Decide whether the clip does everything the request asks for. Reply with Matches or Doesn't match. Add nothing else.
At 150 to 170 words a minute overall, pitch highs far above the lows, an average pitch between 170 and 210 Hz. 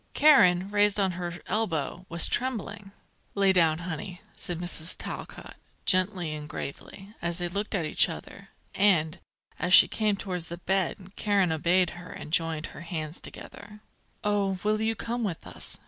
Doesn't match